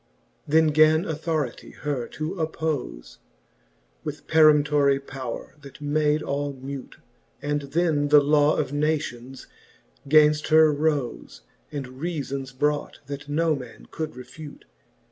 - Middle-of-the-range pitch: Yes, medium, 145 Hz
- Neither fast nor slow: No, slow, 125 wpm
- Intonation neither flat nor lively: No, narrow, 2.0 semitones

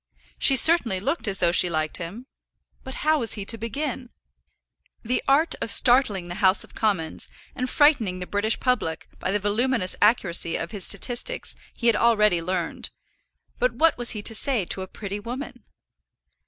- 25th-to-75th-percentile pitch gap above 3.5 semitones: Yes, average, 5.2 semitones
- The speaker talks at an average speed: Yes, average, 175 wpm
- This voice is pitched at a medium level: No, high, 220 Hz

